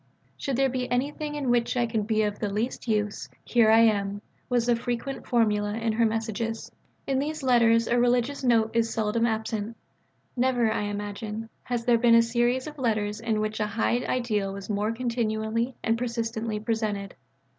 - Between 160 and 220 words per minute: Yes, average, 185 wpm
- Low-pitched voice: No, high, 230 Hz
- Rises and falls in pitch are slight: Yes, narrow, 2.1 semitones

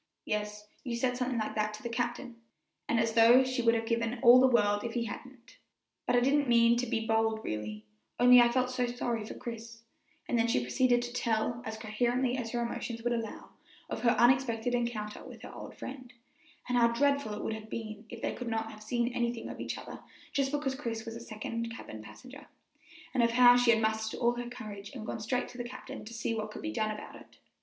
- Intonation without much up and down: Yes, narrow, 1.9 semitones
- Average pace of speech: No, fast, 230 wpm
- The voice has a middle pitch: No, high, 235 Hz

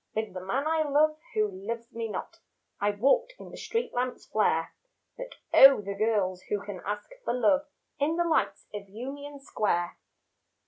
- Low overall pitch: No, high, 230 Hz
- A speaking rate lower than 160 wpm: No, average, 175 wpm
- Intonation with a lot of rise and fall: Yes, wide, 6.0 semitones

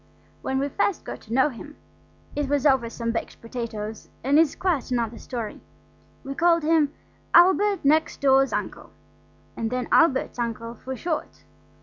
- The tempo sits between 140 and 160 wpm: Yes, average, 155 wpm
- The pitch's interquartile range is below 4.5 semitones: No, average, 4.8 semitones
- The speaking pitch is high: Yes, very high, 270 Hz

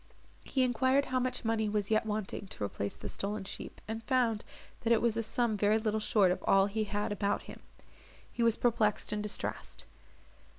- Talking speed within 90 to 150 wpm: No, average, 195 wpm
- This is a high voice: Yes, high, 215 Hz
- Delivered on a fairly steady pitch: Yes, narrow, 2.2 semitones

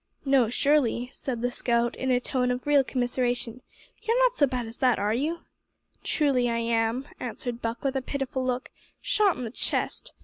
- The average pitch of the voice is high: Yes, very high, 250 Hz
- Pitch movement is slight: Yes, narrow, 2.3 semitones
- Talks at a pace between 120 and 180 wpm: No, average, 190 wpm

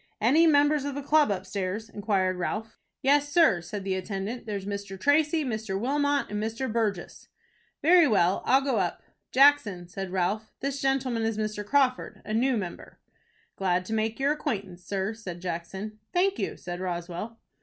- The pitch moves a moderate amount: No, wide, 6.1 semitones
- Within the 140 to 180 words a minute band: Yes, average, 165 wpm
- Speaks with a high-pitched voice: Yes, high, 215 Hz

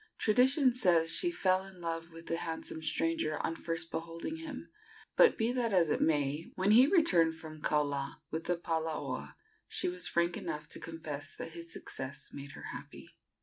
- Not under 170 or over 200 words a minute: Yes, average, 185 wpm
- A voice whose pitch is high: No, medium, 165 Hz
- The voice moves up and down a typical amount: Yes, average, 3.4 semitones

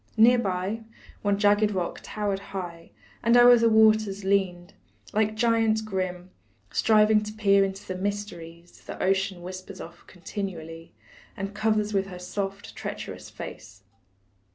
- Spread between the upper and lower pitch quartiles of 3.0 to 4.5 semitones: No, narrow, 2.6 semitones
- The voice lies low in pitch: No, high, 200 Hz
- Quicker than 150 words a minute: No, slow, 135 wpm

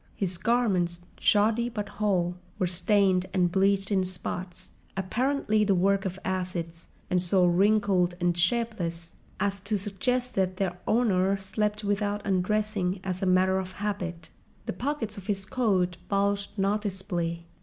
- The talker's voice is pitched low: No, high, 195 Hz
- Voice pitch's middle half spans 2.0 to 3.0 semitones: Yes, narrow, 2.5 semitones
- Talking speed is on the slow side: No, average, 145 wpm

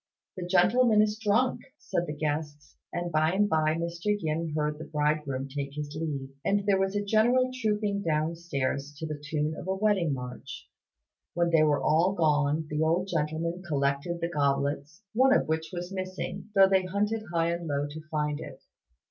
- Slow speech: No, average, 180 wpm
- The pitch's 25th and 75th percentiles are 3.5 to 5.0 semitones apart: Yes, average, 4.3 semitones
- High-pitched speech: No, medium, 165 Hz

